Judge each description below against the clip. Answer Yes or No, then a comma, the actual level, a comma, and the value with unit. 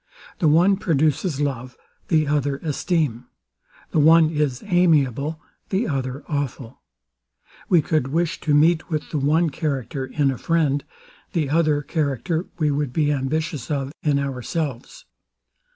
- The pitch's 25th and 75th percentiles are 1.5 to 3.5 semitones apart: Yes, average, 2.8 semitones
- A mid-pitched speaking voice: Yes, medium, 150 Hz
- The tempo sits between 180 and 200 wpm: No, slow, 135 wpm